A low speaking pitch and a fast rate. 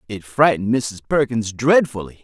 No: low, 115 Hz; slow, 135 wpm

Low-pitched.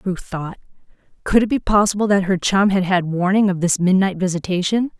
No: high, 190 Hz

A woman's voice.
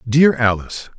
No: male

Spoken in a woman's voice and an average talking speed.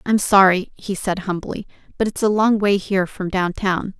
Yes: female; average, 195 wpm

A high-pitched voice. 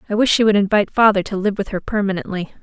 Yes: high, 200 Hz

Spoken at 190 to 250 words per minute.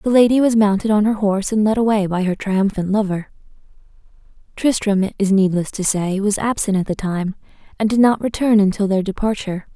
Yes: average, 195 wpm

